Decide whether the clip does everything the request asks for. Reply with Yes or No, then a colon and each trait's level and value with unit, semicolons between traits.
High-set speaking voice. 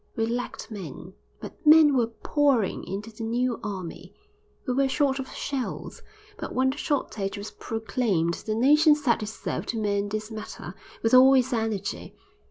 Yes: high, 230 Hz